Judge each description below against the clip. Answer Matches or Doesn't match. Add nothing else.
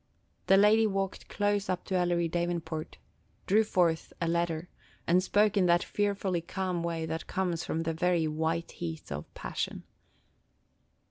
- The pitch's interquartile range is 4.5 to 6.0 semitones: Doesn't match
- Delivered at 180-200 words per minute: Doesn't match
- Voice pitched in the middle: Matches